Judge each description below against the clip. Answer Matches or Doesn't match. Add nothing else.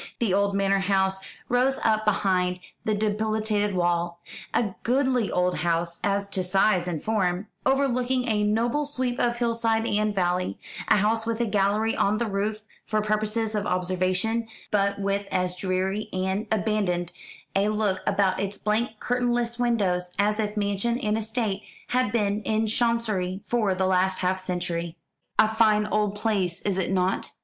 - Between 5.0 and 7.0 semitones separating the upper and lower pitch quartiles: Doesn't match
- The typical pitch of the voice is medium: Doesn't match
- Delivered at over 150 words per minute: Matches